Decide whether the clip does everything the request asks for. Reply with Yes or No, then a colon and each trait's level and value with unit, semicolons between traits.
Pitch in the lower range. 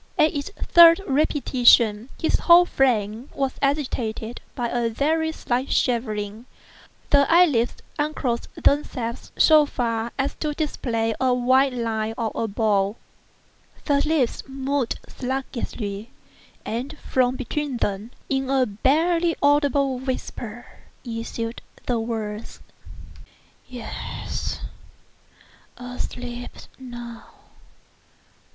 No: very high, 250 Hz